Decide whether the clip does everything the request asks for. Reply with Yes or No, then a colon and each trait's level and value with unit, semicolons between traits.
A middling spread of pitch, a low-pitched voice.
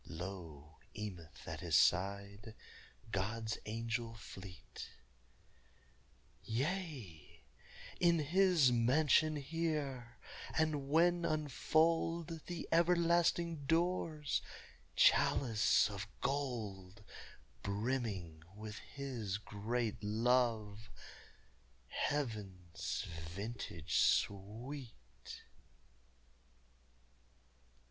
No: wide, 7.3 semitones; low, 115 Hz